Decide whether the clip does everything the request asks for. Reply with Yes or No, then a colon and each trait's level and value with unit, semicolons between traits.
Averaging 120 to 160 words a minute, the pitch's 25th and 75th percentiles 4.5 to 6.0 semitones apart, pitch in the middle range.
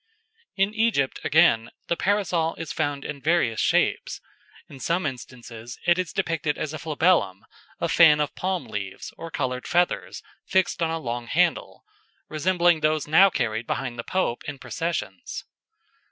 Yes: average, 155 wpm; wide, 5.4 semitones; medium, 155 Hz